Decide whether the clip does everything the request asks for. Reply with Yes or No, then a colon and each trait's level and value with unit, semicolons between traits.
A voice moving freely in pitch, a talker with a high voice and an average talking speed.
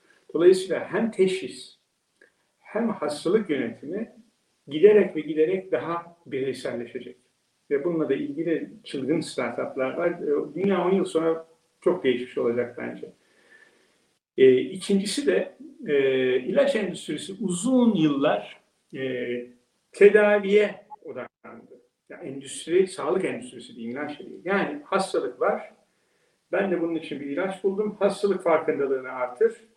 Yes: wide, 7.5 semitones; high, 195 Hz; average, 115 wpm